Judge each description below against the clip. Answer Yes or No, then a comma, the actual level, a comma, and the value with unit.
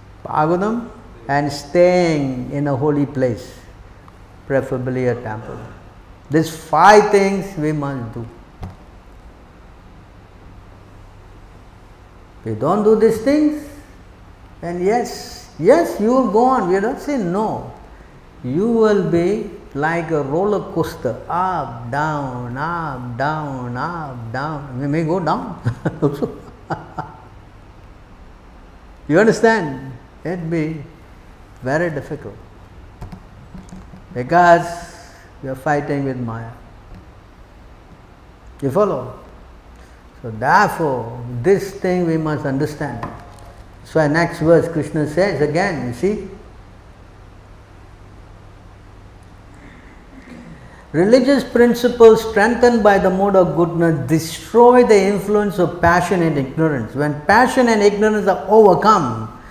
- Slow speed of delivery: Yes, slow, 100 wpm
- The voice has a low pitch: No, medium, 145 Hz